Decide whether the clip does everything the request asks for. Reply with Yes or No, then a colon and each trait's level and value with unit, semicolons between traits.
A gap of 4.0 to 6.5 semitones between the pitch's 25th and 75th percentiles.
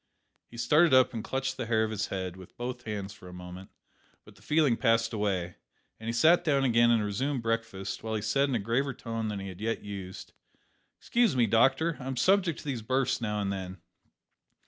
Yes: average, 4.5 semitones